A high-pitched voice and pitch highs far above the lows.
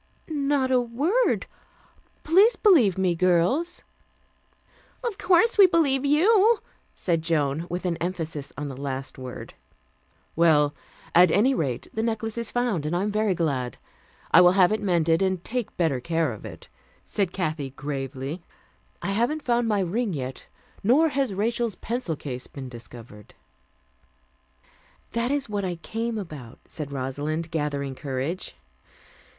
No: medium, 180 Hz; wide, 8.4 semitones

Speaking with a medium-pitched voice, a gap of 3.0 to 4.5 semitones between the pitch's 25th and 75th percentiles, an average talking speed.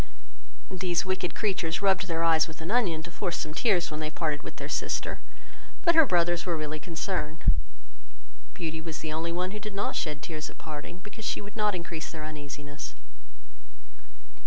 Yes: medium, 170 Hz; average, 3.3 semitones; average, 185 wpm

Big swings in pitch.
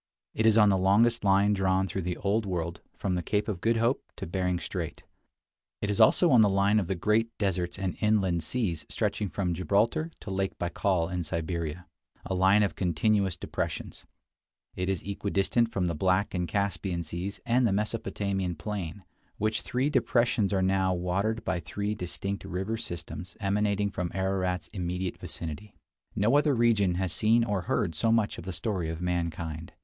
No: average, 3.0 semitones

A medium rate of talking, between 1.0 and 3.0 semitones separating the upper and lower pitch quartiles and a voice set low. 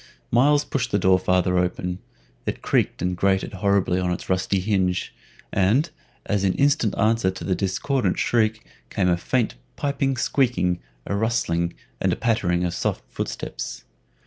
No: average, 155 wpm; average, 4.3 semitones; low, 100 Hz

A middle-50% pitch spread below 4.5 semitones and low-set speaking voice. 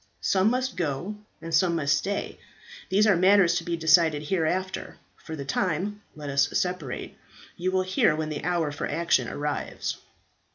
No: average, 3.5 semitones; medium, 170 Hz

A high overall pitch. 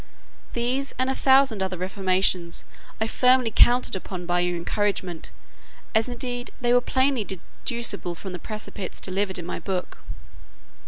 Yes: high, 205 Hz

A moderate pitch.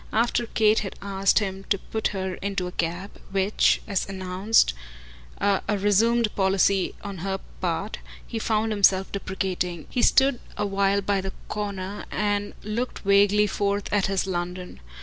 No: high, 200 Hz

